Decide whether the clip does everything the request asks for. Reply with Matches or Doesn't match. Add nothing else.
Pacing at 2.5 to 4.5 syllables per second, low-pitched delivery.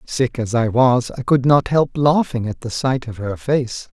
Matches